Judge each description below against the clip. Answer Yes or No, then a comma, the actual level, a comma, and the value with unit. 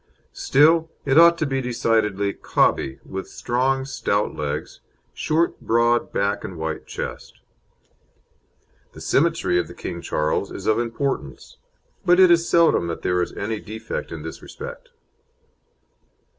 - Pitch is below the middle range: Yes, low, 120 Hz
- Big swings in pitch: Yes, wide, 8.3 semitones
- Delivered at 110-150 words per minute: Yes, average, 140 wpm